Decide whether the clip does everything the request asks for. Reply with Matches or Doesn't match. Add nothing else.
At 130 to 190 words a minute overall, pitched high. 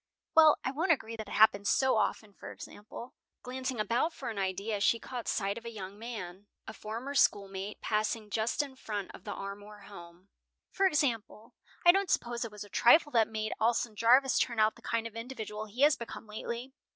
Doesn't match